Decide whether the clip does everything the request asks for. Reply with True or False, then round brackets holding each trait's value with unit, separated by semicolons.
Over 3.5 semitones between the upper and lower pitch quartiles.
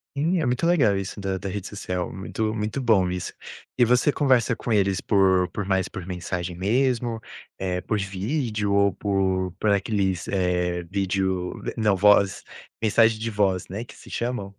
False (3.2 semitones)